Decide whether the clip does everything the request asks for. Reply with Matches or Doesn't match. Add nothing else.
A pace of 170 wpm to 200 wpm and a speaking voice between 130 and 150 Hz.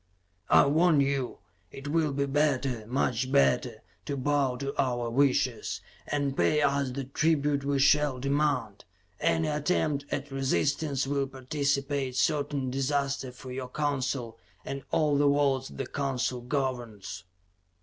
Doesn't match